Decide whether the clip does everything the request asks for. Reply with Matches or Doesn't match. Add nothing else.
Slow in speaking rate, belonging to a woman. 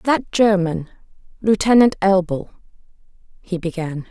Matches